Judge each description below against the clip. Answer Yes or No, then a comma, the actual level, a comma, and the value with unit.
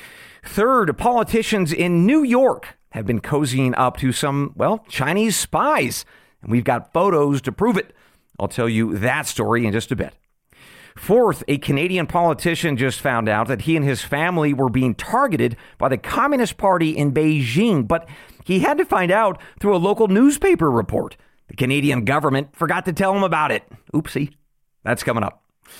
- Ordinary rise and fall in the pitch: No, wide, 6.7 semitones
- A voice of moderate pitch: Yes, medium, 150 Hz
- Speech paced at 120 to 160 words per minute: No, average, 175 wpm